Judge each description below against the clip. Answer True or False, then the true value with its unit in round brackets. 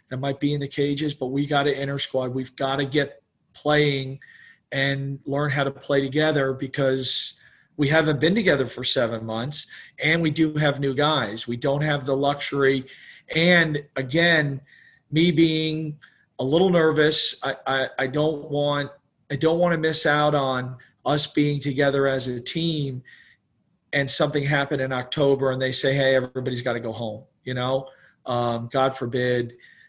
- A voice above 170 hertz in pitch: False (140 Hz)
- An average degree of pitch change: False (2.1 semitones)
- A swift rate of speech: False (175 wpm)